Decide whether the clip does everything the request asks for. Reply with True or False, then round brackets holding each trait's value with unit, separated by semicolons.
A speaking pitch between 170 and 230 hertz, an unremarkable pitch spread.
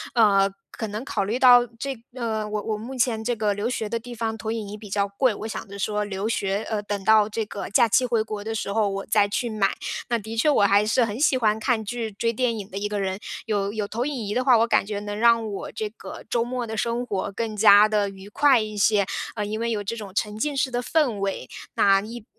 False (220 Hz; 2.3 semitones)